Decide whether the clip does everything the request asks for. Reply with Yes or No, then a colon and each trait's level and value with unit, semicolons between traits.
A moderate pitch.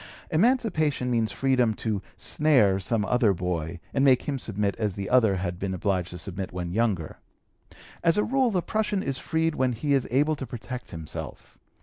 No: low, 120 Hz